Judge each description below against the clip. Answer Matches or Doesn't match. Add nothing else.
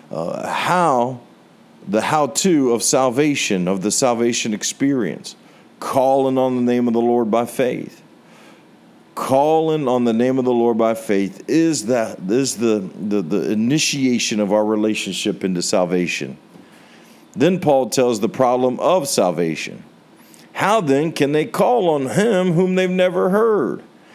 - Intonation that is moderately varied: Doesn't match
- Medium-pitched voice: Doesn't match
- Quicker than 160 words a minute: Doesn't match